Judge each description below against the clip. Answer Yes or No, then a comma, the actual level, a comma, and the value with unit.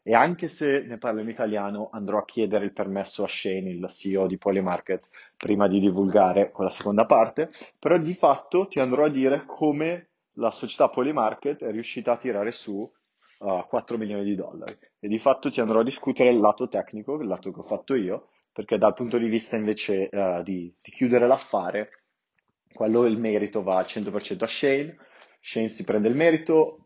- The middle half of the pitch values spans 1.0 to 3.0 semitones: No, average, 4.7 semitones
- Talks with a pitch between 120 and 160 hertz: No, low, 110 Hz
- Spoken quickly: Yes, fast, 190 wpm